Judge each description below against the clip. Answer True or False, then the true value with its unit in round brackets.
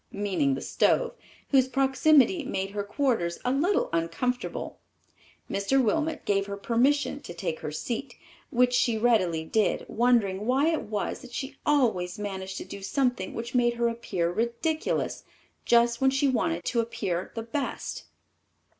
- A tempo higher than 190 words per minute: False (155 wpm)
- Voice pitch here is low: False (235 Hz)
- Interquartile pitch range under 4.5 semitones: False (5.2 semitones)